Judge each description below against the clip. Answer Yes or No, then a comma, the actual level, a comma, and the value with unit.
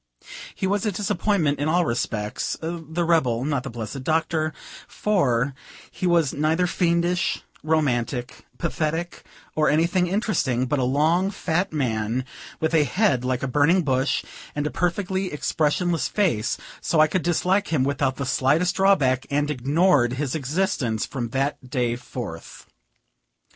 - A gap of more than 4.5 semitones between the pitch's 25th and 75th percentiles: Yes, average, 5.2 semitones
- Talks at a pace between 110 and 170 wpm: Yes, average, 145 wpm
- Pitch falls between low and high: Yes, medium, 150 Hz